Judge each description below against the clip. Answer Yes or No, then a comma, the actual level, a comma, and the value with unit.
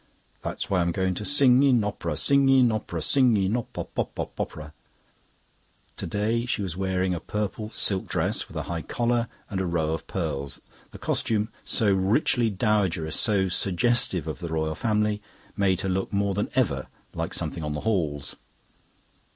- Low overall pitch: Yes, low, 100 Hz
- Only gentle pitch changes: No, average, 4.6 semitones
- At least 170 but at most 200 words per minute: Yes, average, 180 wpm